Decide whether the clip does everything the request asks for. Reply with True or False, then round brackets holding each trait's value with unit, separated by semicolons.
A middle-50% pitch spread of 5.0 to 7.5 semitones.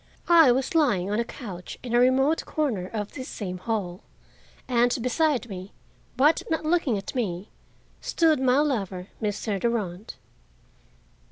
True (5.3 semitones)